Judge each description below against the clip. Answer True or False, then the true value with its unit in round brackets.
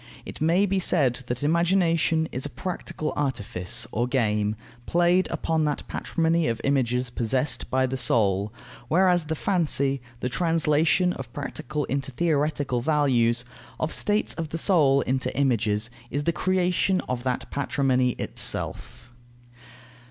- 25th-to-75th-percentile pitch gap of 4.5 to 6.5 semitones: True (4.9 semitones)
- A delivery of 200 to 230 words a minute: False (135 wpm)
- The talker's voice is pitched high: False (140 Hz)